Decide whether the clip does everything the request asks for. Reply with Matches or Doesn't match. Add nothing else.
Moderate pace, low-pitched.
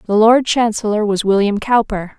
Doesn't match